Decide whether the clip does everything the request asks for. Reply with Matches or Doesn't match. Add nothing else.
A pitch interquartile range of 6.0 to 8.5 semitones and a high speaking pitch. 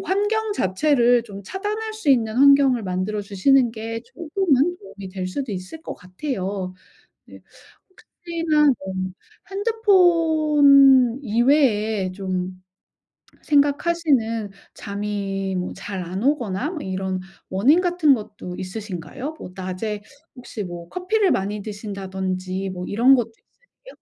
Matches